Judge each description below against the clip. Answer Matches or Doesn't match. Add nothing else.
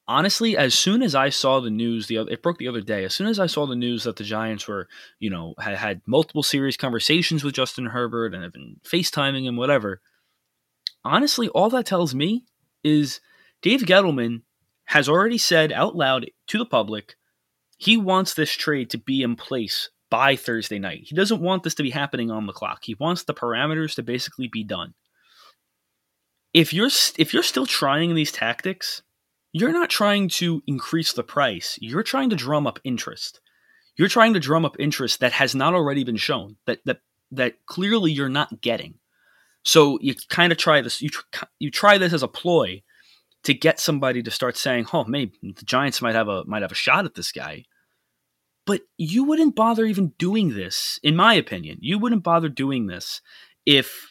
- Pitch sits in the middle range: Matches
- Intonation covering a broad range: Matches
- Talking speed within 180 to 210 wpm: Matches